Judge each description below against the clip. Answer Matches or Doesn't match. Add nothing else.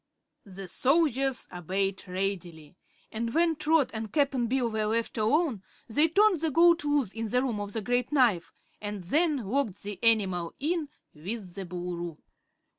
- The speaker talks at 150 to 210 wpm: Matches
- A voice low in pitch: Doesn't match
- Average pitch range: Doesn't match